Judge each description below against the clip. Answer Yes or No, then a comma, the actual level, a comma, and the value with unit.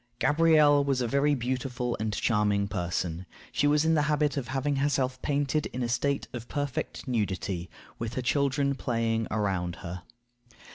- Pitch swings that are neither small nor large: Yes, average, 4.7 semitones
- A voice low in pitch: Yes, low, 130 Hz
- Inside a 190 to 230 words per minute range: No, average, 160 wpm